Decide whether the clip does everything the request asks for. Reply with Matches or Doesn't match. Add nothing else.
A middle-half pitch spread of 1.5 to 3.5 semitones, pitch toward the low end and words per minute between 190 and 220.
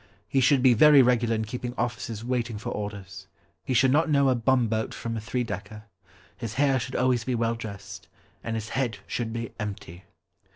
Matches